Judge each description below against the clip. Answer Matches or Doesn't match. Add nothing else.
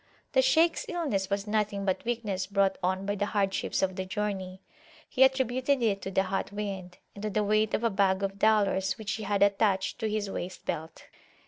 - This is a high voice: Matches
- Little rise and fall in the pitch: Matches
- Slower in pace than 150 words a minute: Doesn't match